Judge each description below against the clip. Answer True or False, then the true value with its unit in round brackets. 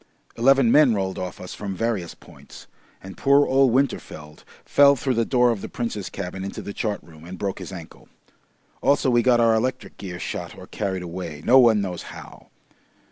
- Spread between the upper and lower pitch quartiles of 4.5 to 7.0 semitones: True (5.2 semitones)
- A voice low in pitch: True (105 Hz)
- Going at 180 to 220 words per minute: True (190 wpm)